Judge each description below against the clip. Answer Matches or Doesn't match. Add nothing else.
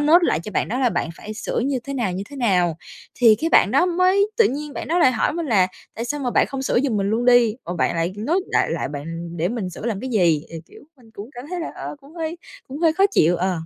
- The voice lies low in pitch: Doesn't match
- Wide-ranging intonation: Matches